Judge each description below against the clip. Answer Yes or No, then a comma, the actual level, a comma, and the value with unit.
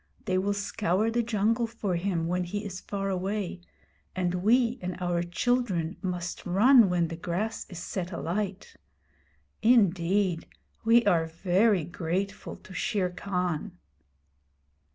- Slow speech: Yes, slow, 130 wpm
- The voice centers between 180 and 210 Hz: Yes, high, 190 Hz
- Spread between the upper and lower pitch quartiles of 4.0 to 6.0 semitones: No, average, 3.3 semitones